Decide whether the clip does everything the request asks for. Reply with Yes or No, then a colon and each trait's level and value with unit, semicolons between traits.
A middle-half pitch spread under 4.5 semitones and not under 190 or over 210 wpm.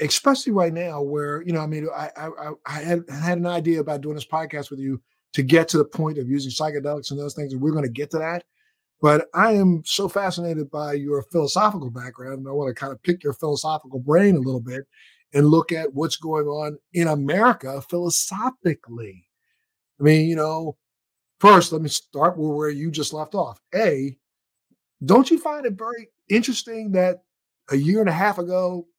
Yes: average, 3.7 semitones; average, 200 wpm